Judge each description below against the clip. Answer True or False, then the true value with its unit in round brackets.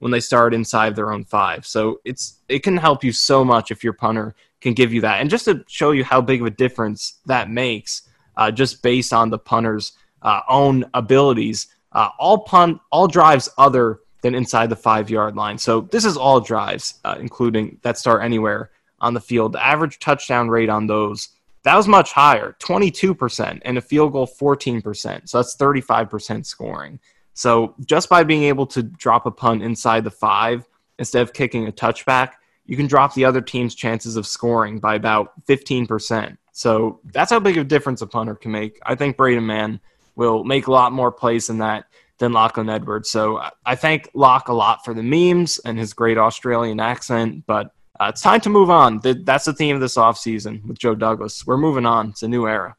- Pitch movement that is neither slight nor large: True (3.3 semitones)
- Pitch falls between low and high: False (120 Hz)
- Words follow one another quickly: True (210 wpm)